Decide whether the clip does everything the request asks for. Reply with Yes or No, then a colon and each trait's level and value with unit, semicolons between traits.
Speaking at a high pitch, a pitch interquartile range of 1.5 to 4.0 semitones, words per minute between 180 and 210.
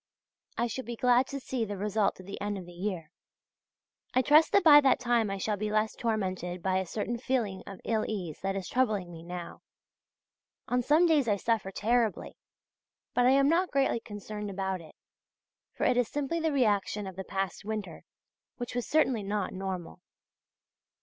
No: high, 215 Hz; average, 4.5 semitones; average, 190 wpm